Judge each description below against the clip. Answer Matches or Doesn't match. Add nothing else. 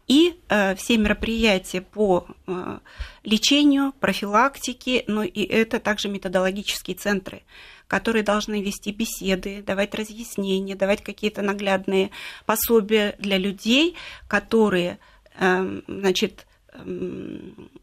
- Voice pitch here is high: Matches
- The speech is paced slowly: Matches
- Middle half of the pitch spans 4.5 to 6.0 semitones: Doesn't match